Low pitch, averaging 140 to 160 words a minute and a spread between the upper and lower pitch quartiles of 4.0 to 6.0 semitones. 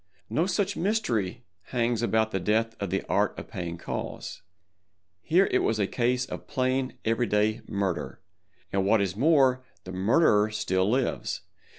Yes: low, 110 Hz; average, 155 wpm; average, 4.7 semitones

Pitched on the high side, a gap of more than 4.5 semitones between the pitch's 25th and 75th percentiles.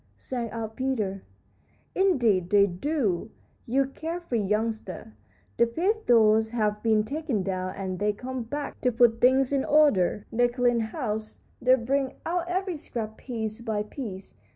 No: high, 230 Hz; average, 4.2 semitones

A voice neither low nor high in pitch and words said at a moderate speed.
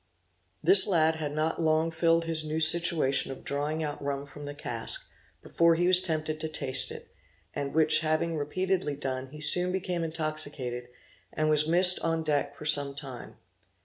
Yes: medium, 155 Hz; average, 175 wpm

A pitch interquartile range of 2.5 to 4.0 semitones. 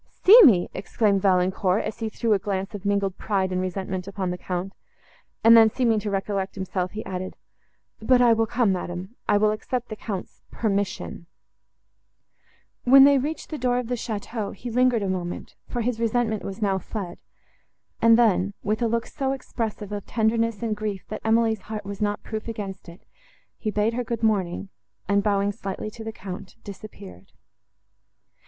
Yes: average, 3.0 semitones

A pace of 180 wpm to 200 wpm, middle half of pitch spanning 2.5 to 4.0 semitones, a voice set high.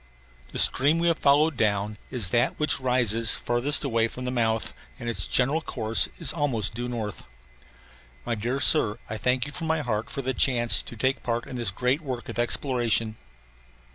No: average, 190 wpm; average, 3.3 semitones; low, 120 Hz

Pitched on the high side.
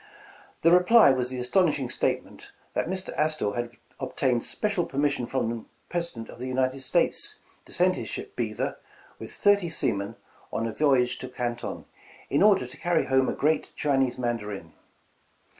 No: low, 130 Hz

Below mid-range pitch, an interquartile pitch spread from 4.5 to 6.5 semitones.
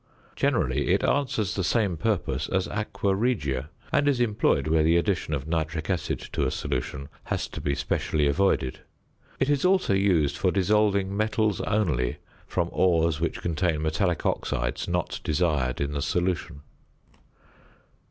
Yes: very low, 85 Hz; average, 5.1 semitones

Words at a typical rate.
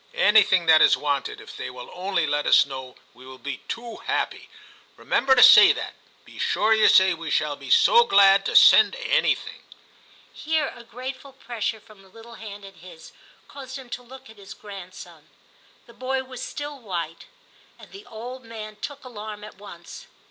Yes: average, 185 wpm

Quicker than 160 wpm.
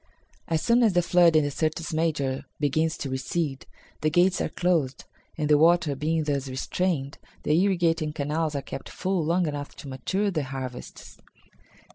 Yes: average, 170 wpm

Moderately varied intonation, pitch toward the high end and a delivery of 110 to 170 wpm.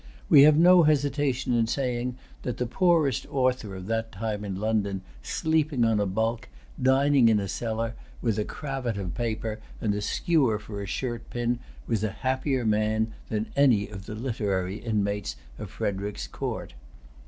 No: average, 3.9 semitones; low, 115 Hz; average, 165 wpm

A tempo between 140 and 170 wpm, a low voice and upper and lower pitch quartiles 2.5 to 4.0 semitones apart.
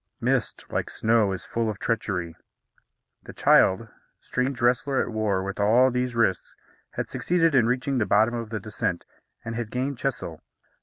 Yes: average, 165 wpm; low, 115 Hz; average, 3.6 semitones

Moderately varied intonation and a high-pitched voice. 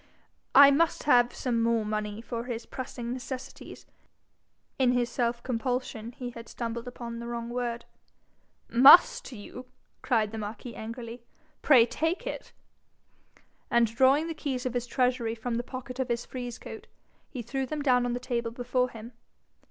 No: narrow, 1.6 semitones; high, 245 Hz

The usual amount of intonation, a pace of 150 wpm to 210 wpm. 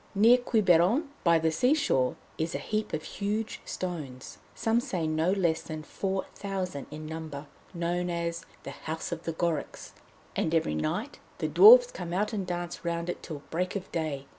Yes: average, 4.0 semitones; average, 180 wpm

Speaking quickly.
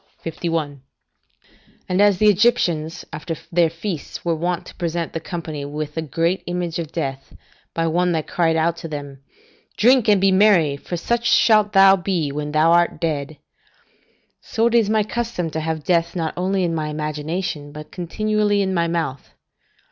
No: average, 175 wpm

